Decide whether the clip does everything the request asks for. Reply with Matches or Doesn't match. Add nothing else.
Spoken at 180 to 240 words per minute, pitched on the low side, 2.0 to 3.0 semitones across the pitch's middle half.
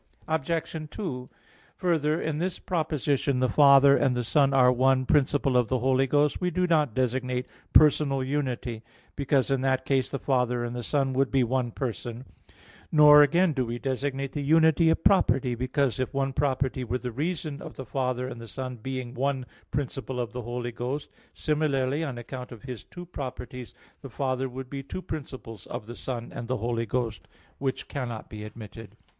Matches